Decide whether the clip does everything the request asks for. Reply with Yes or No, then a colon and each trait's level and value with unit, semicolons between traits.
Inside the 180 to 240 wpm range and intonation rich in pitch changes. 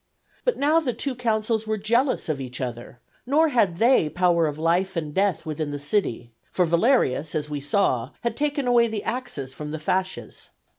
Yes: average, 190 wpm; wide, 8.0 semitones